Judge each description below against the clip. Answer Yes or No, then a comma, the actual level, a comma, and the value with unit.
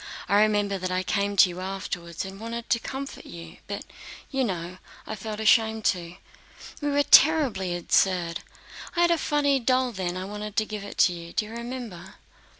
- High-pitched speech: Yes, high, 205 Hz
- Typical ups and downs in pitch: Yes, average, 4.3 semitones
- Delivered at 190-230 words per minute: Yes, average, 195 wpm